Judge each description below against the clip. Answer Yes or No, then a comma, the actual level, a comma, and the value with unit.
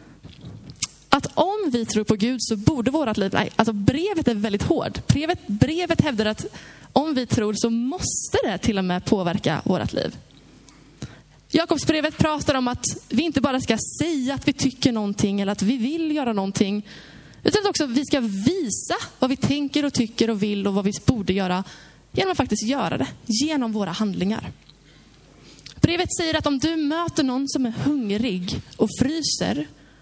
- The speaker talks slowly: No, average, 180 wpm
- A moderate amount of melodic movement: No, wide, 5.7 semitones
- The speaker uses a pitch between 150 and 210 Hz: No, very high, 250 Hz